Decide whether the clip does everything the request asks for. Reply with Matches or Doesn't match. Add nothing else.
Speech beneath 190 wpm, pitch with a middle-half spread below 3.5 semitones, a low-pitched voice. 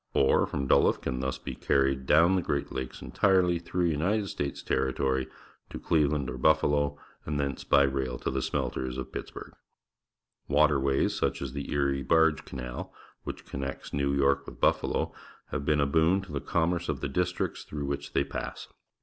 Matches